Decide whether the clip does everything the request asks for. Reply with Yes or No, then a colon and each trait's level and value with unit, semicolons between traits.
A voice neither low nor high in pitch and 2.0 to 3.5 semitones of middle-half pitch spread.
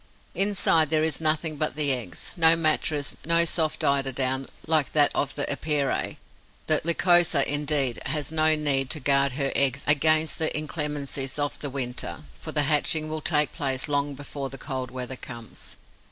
Yes: medium, 145 Hz; narrow, 2.4 semitones